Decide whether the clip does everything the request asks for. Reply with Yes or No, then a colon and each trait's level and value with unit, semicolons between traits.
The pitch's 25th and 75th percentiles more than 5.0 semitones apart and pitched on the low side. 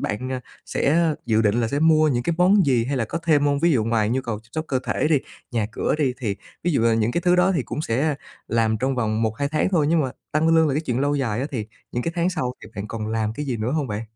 Yes: wide, 5.4 semitones; low, 130 Hz